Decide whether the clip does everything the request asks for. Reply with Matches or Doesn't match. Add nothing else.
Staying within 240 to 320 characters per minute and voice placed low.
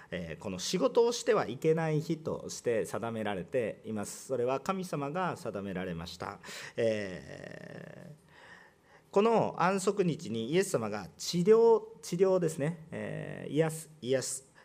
Doesn't match